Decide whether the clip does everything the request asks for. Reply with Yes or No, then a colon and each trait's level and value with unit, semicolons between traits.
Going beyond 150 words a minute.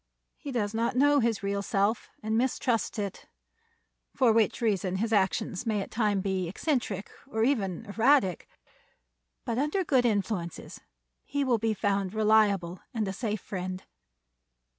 No: average, 145 wpm